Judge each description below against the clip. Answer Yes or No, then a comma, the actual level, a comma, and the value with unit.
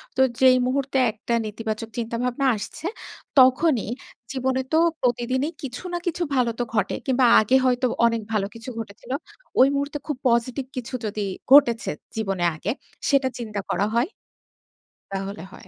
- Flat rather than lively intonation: No, average, 3.0 semitones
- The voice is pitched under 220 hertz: No, high, 245 Hz